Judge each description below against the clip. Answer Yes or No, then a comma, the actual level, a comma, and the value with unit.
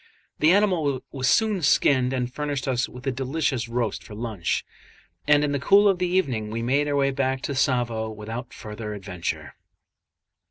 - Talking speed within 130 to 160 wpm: No, average, 175 wpm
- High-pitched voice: No, low, 130 Hz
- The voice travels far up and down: No, average, 4.0 semitones